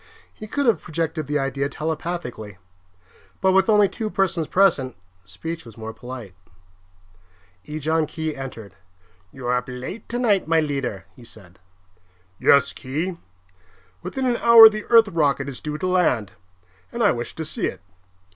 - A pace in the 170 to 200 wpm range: No, average, 155 wpm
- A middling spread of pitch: No, wide, 6.9 semitones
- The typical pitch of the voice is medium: Yes, medium, 155 Hz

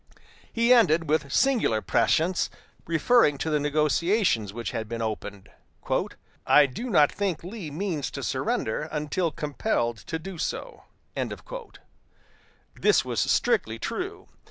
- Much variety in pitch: Yes, wide, 6.0 semitones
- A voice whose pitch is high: No, medium, 155 Hz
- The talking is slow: Yes, slow, 125 wpm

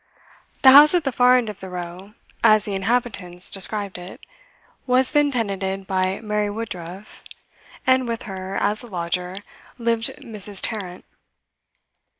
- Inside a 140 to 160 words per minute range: Yes, average, 145 wpm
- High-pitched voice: Yes, high, 205 Hz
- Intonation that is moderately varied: Yes, average, 3.9 semitones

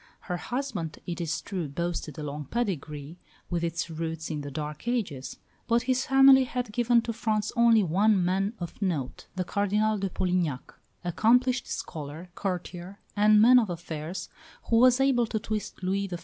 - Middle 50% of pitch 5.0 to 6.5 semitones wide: Yes, wide, 5.6 semitones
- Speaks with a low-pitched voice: No, high, 190 Hz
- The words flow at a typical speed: Yes, average, 170 wpm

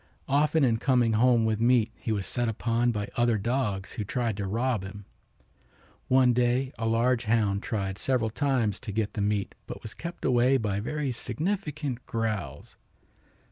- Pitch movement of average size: Yes, average, 3.0 semitones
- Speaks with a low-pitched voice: Yes, low, 115 Hz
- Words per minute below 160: No, average, 170 wpm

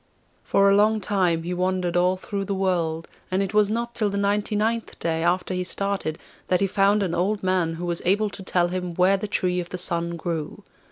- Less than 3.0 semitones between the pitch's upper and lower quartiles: Yes, narrow, 2.4 semitones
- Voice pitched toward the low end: No, medium, 185 Hz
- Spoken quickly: Yes, fast, 225 wpm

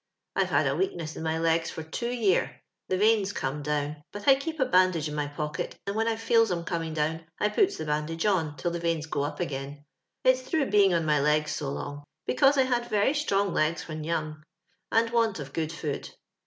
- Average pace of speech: No, fast, 225 wpm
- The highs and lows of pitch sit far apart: Yes, wide, 6.5 semitones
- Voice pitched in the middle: Yes, medium, 170 Hz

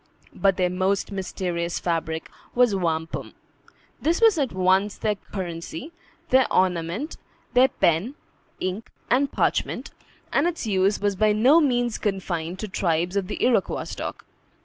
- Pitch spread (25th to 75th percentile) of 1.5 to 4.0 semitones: No, wide, 5.4 semitones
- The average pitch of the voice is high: Yes, high, 195 Hz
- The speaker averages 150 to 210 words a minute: No, average, 140 wpm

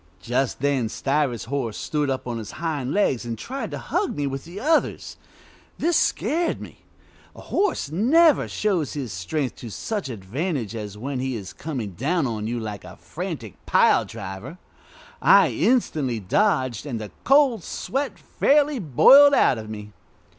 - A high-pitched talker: No, low, 135 Hz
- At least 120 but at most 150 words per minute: No, average, 160 wpm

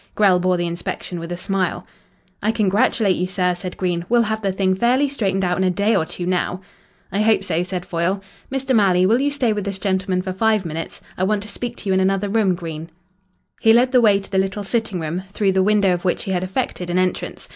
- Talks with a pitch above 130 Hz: Yes, high, 190 Hz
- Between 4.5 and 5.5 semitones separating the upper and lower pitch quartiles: No, average, 2.8 semitones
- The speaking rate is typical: No, fast, 245 wpm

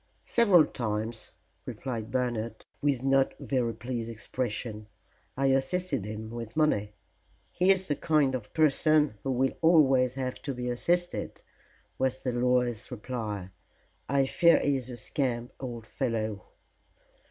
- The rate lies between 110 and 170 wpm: Yes, slow, 135 wpm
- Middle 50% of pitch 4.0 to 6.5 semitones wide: No, average, 3.3 semitones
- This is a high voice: No, low, 125 Hz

